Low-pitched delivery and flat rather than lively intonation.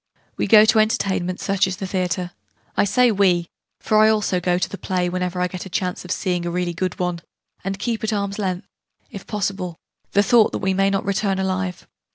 No: high, 190 Hz; narrow, 2.0 semitones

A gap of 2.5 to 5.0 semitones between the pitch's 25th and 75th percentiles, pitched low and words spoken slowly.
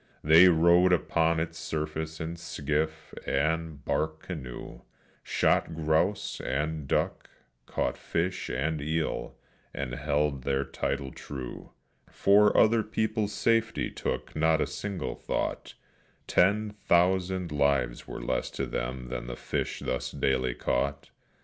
Yes: average, 4.1 semitones; very low, 80 Hz; slow, 125 wpm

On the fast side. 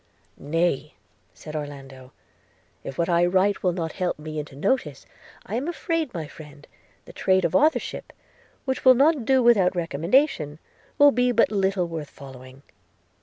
No: average, 155 wpm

